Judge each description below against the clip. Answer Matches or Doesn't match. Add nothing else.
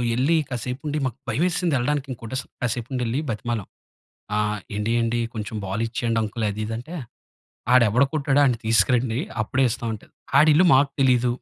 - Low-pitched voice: Matches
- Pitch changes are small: Doesn't match